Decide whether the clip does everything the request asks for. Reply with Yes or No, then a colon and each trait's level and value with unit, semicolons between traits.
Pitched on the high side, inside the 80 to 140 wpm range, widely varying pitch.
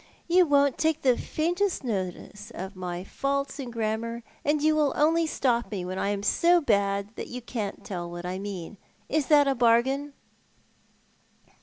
No: high, 235 Hz; average, 170 wpm; wide, 6.5 semitones